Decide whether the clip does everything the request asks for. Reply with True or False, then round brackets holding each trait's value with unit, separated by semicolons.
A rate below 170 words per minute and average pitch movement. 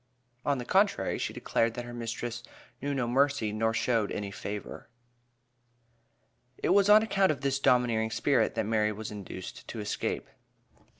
True (160 wpm; 4.3 semitones)